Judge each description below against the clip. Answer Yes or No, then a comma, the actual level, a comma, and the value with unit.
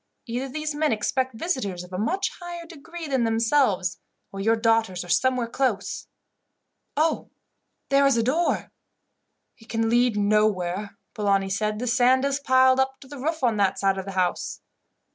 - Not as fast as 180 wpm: Yes, average, 170 wpm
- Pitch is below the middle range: No, high, 235 Hz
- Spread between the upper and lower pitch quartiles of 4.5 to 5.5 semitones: Yes, average, 5.2 semitones